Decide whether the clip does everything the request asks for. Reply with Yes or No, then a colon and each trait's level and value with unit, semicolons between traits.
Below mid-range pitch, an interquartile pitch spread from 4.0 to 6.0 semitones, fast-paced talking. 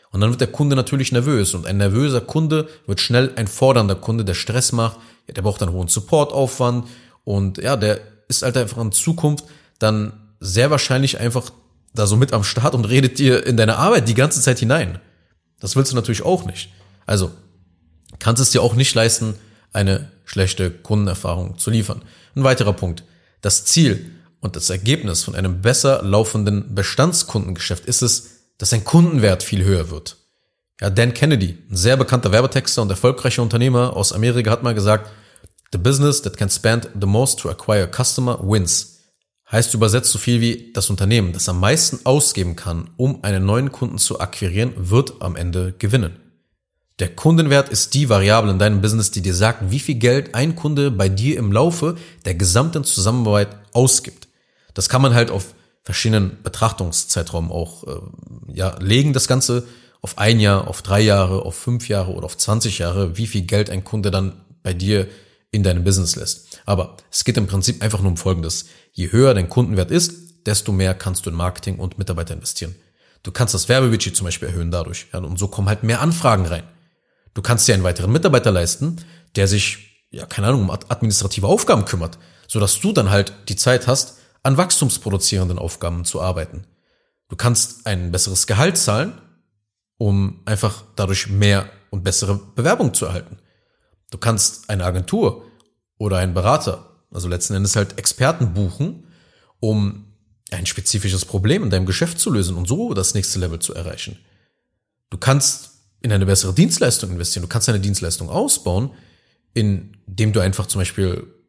No: low, 105 Hz; average, 4.5 semitones; average, 180 wpm